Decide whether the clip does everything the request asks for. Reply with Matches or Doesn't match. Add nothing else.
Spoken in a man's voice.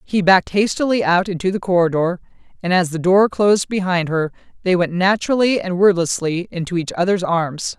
Doesn't match